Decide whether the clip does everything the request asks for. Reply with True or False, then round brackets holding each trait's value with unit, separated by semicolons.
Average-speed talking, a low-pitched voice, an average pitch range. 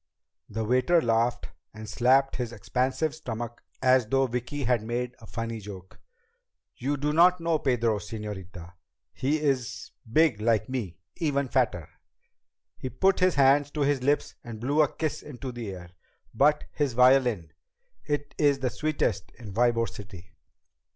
True (150 wpm; 125 Hz; 4.3 semitones)